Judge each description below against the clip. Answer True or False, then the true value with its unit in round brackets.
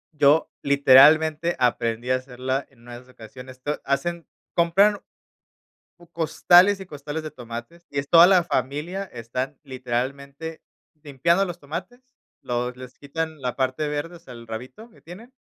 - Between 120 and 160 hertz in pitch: True (140 Hz)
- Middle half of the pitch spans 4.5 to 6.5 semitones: True (4.9 semitones)